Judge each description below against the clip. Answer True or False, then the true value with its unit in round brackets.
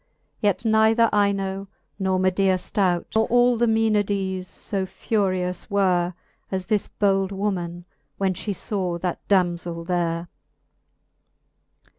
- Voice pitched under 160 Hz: False (190 Hz)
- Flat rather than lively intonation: True (2.2 semitones)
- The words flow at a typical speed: False (115 wpm)